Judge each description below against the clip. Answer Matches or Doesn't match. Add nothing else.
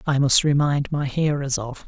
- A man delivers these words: Matches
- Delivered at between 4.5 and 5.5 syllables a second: Matches